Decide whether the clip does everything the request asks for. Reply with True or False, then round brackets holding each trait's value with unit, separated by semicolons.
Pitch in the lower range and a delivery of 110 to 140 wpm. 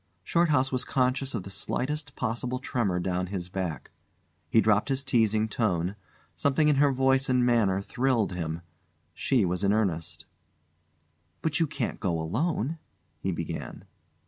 False (115 Hz; 150 wpm)